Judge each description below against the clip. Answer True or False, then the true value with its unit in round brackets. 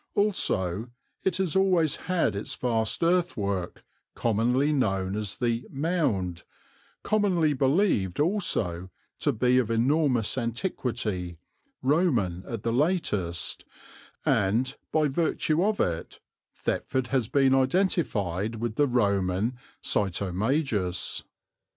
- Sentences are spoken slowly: True (105 wpm)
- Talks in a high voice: False (120 Hz)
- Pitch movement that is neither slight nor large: False (7.5 semitones)